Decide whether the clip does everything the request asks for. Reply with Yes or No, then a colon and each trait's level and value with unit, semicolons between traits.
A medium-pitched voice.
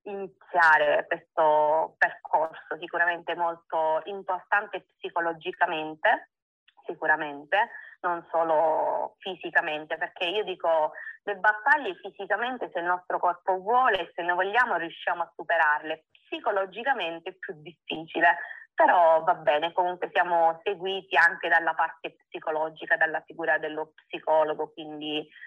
Yes: medium, 175 Hz